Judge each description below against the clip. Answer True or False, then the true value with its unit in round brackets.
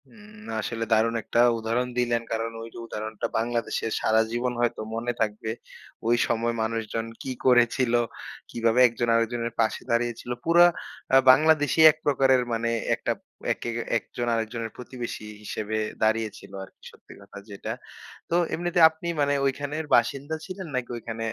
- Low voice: True (120 Hz)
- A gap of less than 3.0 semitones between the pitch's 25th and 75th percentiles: True (2.4 semitones)